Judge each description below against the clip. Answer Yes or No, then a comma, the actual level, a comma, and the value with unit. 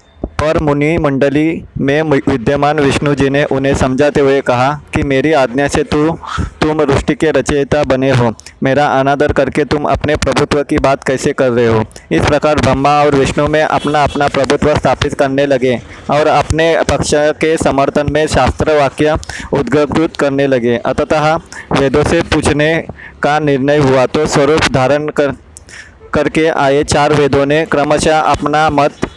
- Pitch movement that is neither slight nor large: No, narrow, 1.6 semitones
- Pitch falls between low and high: Yes, medium, 145 Hz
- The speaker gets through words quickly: No, average, 160 wpm